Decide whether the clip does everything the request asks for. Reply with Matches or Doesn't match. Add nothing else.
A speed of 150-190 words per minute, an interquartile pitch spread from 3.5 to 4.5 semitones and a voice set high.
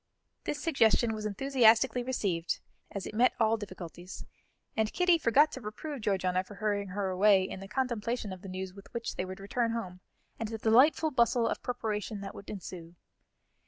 Matches